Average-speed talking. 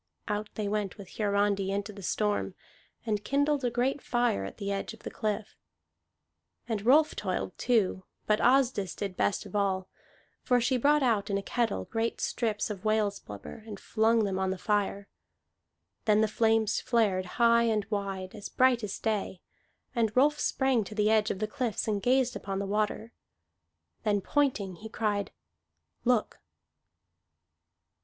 Yes: average, 165 wpm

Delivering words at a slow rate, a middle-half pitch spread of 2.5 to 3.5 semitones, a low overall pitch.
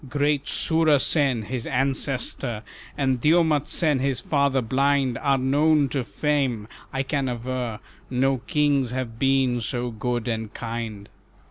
Yes: slow, 125 wpm; average, 2.8 semitones; low, 130 Hz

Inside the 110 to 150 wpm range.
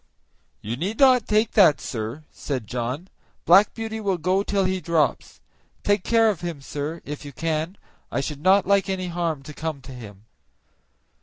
No: average, 175 wpm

